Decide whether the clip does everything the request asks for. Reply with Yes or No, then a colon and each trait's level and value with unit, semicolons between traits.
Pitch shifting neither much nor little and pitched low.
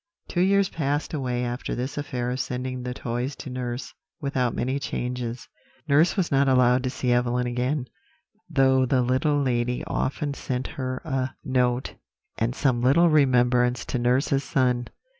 No: narrow, 2.0 semitones; low, 130 Hz